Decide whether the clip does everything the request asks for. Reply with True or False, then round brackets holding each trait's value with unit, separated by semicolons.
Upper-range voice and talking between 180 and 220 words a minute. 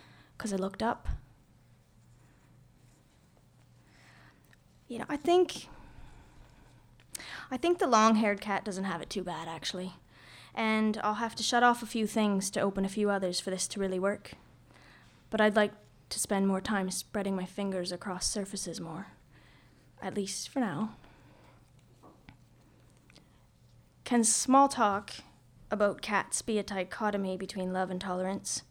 False (195 Hz; 140 wpm)